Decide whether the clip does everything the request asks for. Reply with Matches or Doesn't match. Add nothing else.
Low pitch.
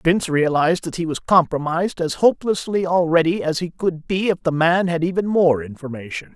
Doesn't match